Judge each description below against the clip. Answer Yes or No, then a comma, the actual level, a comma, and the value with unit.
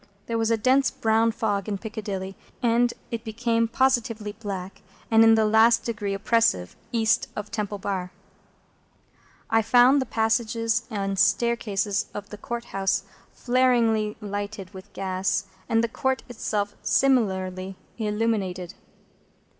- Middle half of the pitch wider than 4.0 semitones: No, narrow, 2.6 semitones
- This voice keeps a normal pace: No, slow, 130 wpm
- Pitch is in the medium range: No, high, 220 Hz